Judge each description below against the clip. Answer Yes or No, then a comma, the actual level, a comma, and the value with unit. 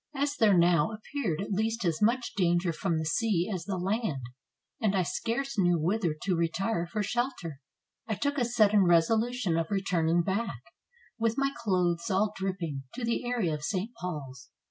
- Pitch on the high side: Yes, high, 195 Hz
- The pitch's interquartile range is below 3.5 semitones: No, average, 5.0 semitones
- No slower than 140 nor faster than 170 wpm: No, average, 180 wpm